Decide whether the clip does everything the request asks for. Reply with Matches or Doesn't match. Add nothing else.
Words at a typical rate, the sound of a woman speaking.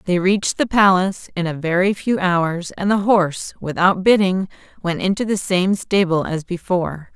Matches